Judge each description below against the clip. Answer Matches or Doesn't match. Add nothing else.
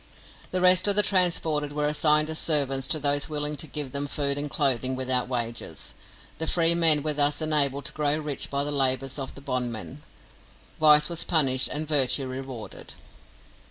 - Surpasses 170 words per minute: Matches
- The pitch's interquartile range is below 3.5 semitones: Matches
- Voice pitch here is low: Doesn't match